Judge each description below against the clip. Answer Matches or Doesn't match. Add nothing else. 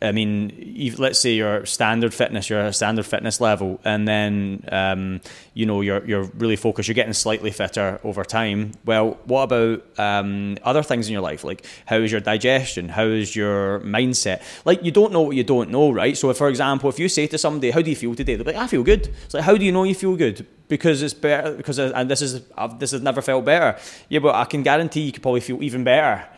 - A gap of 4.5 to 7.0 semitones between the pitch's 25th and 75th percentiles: Matches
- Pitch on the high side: Doesn't match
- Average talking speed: Doesn't match